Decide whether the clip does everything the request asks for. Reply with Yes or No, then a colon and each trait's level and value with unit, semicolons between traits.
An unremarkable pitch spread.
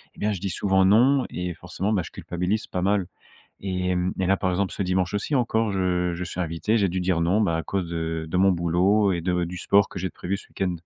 No: narrow, 2.1 semitones